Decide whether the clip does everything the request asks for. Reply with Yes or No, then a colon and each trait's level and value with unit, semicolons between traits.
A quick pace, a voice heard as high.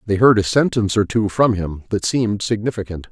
No: fast, 210 wpm; low, 105 Hz